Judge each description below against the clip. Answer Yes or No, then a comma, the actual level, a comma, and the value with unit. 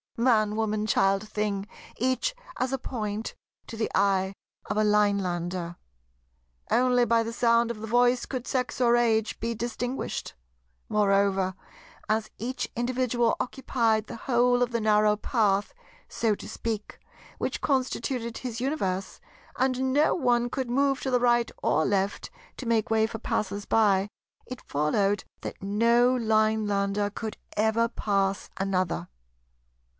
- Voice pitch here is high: Yes, high, 225 Hz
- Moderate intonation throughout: Yes, average, 3.1 semitones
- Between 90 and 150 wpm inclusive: Yes, average, 140 wpm